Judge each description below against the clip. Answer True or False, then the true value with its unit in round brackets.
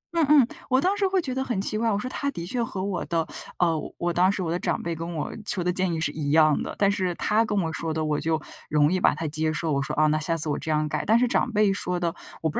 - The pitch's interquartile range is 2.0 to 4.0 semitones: False (4.9 semitones)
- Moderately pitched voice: True (175 Hz)